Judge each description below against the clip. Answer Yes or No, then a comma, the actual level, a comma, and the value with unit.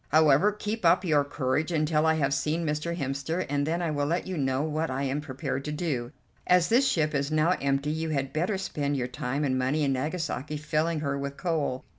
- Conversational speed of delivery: No, fast, 220 wpm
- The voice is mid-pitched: Yes, medium, 150 Hz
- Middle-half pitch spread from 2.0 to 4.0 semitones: Yes, average, 2.8 semitones